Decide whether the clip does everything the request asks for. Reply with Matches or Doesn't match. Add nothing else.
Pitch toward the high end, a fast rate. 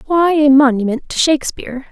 Doesn't match